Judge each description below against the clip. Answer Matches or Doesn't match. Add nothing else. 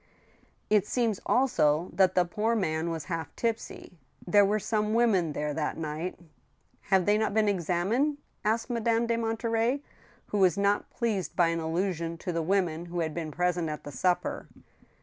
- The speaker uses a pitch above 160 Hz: Matches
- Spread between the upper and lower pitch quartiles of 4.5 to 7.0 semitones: Matches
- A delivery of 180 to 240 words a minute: Matches